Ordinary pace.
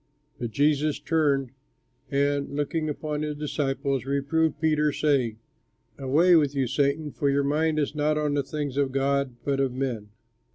Yes: average, 160 wpm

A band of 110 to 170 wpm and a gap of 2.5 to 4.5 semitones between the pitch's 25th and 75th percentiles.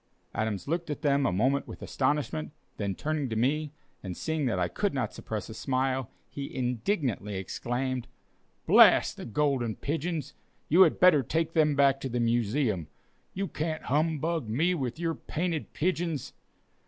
No: average, 160 wpm; average, 5.0 semitones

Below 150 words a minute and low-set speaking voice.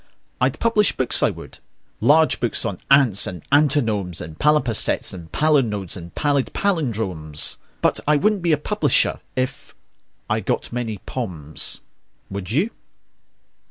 Yes: slow, 135 wpm; low, 120 Hz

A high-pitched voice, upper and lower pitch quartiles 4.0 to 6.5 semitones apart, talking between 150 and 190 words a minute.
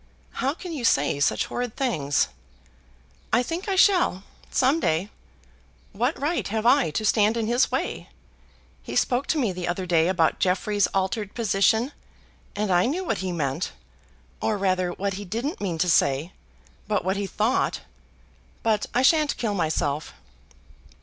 Yes: high, 205 Hz; wide, 5.5 semitones; average, 160 wpm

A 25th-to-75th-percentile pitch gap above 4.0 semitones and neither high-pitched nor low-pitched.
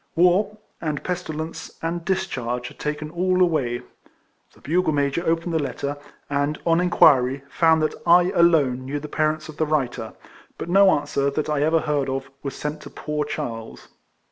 No: average, 3.3 semitones; medium, 155 Hz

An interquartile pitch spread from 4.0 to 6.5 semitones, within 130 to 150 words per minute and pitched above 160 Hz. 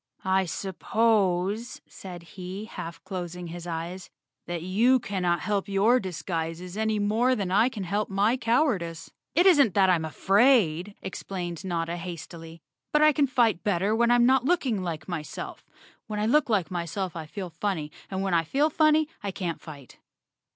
No: average, 4.6 semitones; average, 170 wpm; high, 190 Hz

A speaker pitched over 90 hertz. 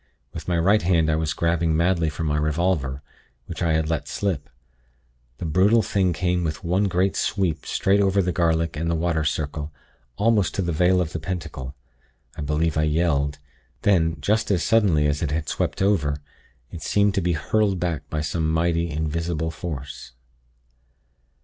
No: very low, 85 Hz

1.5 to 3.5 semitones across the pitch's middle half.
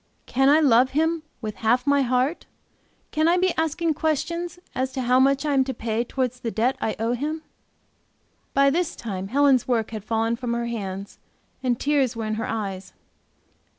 No: average, 4.3 semitones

